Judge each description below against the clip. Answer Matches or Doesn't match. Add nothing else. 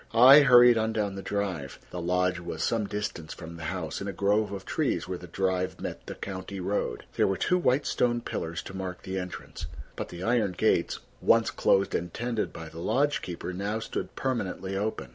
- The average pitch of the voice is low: Matches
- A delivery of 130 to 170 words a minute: Doesn't match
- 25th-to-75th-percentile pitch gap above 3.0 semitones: Matches